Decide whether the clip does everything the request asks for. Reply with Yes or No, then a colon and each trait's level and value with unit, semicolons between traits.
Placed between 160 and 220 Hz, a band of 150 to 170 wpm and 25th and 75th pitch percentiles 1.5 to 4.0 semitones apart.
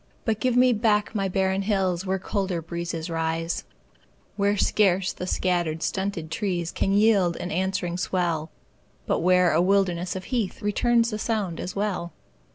Yes: high, 190 Hz; average, 160 wpm; average, 3.0 semitones